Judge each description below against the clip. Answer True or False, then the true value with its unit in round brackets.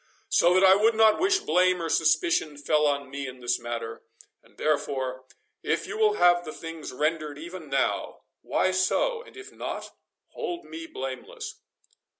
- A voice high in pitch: False (165 Hz)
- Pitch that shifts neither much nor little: False (5.8 semitones)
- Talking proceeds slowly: False (155 wpm)